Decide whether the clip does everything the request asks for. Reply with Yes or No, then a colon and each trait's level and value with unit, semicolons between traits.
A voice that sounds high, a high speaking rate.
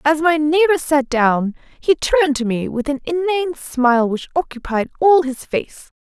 No: very high, 290 Hz; average, 180 wpm